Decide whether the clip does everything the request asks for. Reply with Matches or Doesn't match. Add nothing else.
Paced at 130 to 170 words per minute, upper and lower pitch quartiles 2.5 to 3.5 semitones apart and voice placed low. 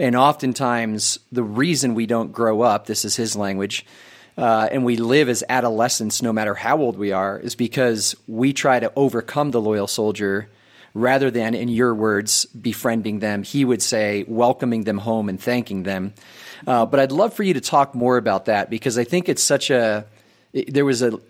Doesn't match